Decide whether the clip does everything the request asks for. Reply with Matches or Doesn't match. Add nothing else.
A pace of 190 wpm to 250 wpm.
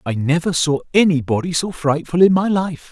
Matches